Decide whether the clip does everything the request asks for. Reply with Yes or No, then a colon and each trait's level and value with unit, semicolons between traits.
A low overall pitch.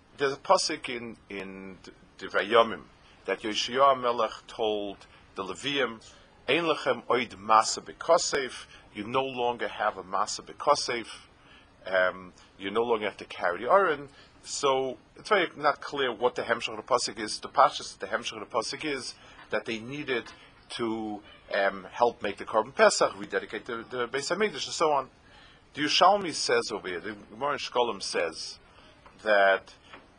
Yes: low, 110 Hz